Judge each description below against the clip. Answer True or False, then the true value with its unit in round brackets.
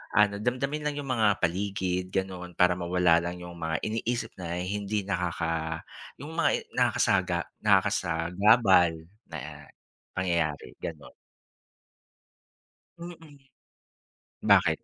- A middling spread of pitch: True (3.8 semitones)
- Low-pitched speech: True (95 Hz)